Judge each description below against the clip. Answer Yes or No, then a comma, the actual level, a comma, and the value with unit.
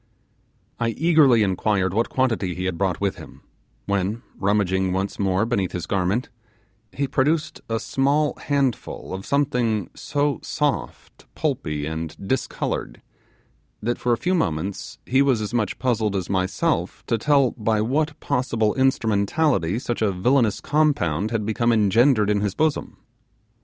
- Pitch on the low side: Yes, low, 110 Hz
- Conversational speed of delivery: Yes, average, 145 wpm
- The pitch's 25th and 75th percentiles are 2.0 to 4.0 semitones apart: No, wide, 5.5 semitones